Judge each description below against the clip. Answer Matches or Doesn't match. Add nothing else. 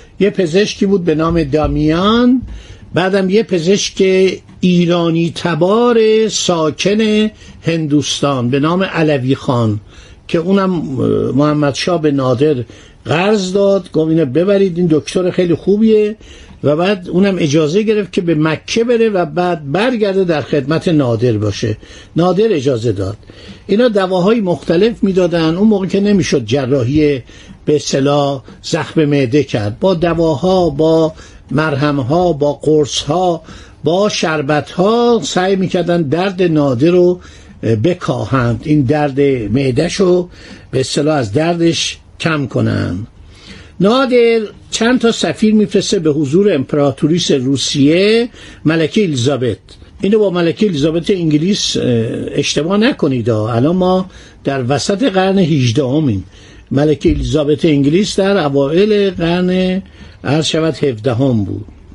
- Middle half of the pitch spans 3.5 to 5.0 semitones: Doesn't match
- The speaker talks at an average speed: Matches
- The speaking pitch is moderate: Matches